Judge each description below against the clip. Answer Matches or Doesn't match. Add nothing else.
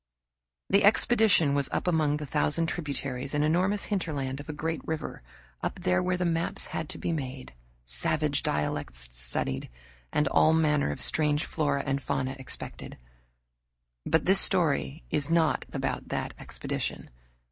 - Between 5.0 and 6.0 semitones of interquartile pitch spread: Doesn't match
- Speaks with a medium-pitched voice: Matches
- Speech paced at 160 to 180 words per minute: Doesn't match